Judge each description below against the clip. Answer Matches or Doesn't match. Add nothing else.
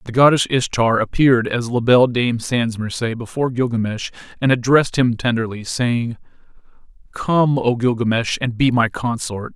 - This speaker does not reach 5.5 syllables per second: Matches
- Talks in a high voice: Doesn't match